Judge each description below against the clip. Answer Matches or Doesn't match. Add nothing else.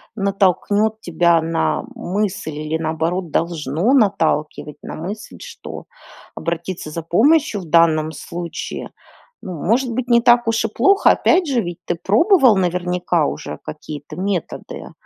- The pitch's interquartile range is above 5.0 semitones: Matches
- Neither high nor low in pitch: Matches